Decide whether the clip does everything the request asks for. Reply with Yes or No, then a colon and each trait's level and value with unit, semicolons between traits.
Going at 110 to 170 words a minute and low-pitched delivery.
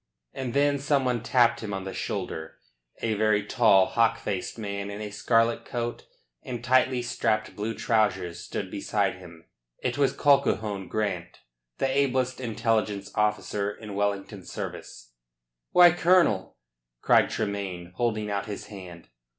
Yes: average, 140 wpm; low, 105 Hz